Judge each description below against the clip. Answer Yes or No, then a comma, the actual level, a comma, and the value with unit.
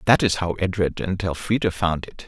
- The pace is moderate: No, fast, 210 wpm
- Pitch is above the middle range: No, very low, 90 Hz